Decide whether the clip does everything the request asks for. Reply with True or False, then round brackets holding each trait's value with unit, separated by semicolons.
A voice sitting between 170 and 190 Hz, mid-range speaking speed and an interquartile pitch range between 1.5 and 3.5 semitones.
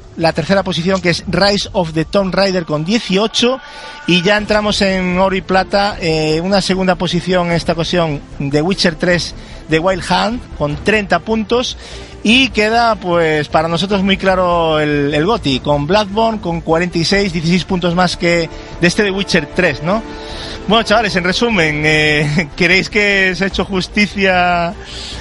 True (185 Hz; 165 wpm; 3.2 semitones)